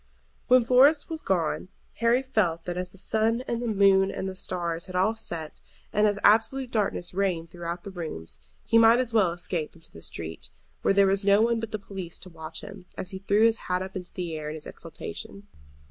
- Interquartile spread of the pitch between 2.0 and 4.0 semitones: No, average, 4.4 semitones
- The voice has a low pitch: No, high, 195 Hz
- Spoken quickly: Yes, fast, 220 wpm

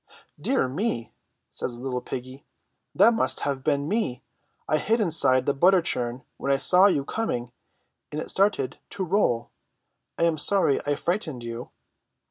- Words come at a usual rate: Yes, average, 160 wpm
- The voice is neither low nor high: Yes, medium, 145 Hz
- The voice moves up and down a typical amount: No, wide, 6.8 semitones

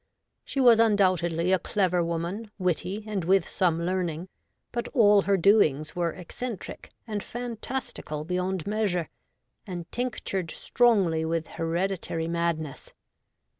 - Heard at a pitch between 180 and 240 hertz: Yes, medium, 185 Hz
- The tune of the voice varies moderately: Yes, average, 3.8 semitones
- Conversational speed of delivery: No, slow, 120 wpm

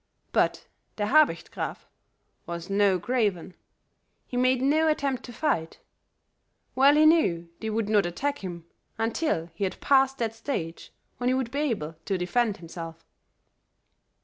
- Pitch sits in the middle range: No, high, 225 Hz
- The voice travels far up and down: Yes, wide, 7.1 semitones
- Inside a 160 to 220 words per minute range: No, average, 150 wpm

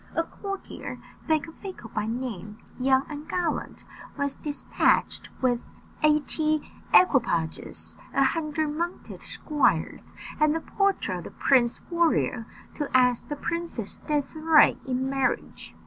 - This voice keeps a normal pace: No, slow, 115 wpm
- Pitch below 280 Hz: No, very high, 295 Hz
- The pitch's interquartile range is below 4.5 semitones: Yes, average, 4.1 semitones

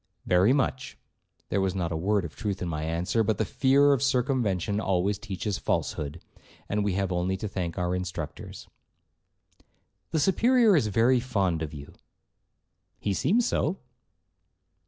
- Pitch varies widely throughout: Yes, wide, 6.2 semitones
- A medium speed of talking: Yes, average, 155 wpm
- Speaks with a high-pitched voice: No, low, 100 Hz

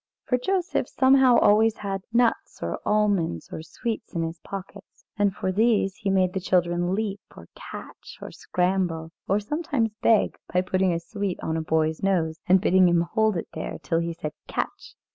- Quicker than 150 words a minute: Yes, average, 180 wpm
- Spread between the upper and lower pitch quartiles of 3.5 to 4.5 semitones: Yes, average, 4.2 semitones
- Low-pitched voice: No, high, 190 Hz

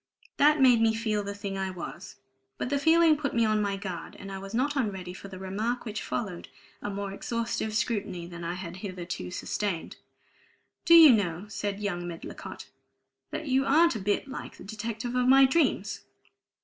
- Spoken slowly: No, average, 190 wpm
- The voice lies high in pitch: Yes, high, 210 Hz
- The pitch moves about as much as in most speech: Yes, average, 4.6 semitones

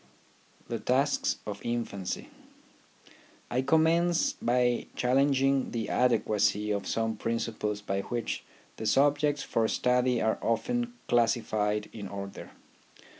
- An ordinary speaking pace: No, slow, 110 wpm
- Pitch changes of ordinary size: Yes, average, 4.2 semitones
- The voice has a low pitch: Yes, low, 120 Hz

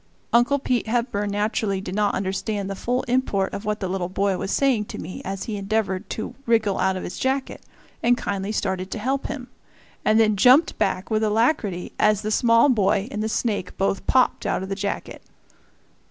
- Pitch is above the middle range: Yes, high, 210 Hz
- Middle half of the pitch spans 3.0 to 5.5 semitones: Yes, average, 3.3 semitones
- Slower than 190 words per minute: No, average, 195 wpm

